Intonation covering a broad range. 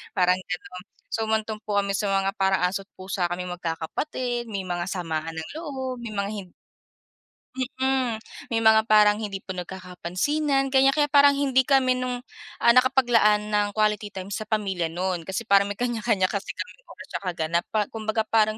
No: average, 4.6 semitones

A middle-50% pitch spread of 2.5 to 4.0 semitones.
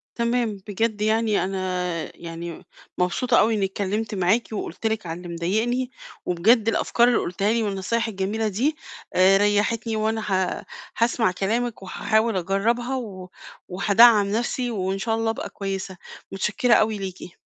Yes: average, 3.3 semitones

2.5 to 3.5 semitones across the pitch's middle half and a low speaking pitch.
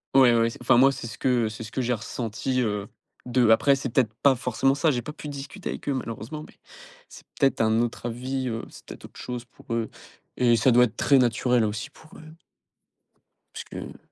Yes: average, 2.8 semitones; low, 125 Hz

